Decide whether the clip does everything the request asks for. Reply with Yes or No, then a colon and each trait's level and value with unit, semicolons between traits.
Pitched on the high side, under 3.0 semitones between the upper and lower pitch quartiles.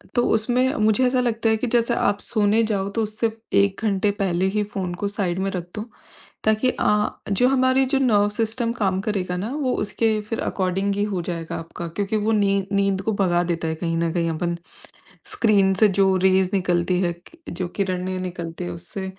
No: high, 200 Hz; average, 3.3 semitones